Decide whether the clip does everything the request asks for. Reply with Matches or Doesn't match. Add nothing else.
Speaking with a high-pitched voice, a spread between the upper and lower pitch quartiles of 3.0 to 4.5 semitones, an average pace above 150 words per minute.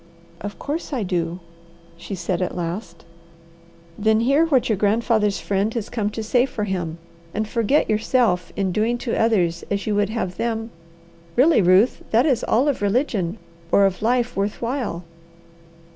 Matches